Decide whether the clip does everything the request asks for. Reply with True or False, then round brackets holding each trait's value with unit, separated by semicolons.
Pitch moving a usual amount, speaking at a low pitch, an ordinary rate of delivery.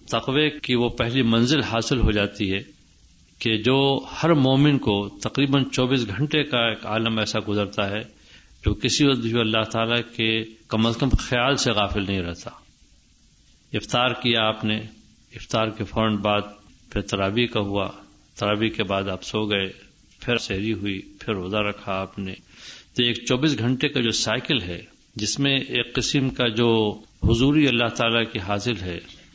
True (3.2 semitones; 110 Hz; 170 wpm)